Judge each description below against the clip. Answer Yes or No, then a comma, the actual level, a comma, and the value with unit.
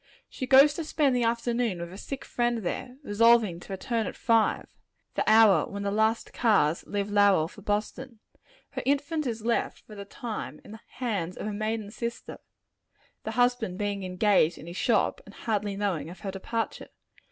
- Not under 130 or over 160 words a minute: No, average, 185 wpm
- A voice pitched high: Yes, high, 220 Hz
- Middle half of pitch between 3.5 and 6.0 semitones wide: No, average, 3.0 semitones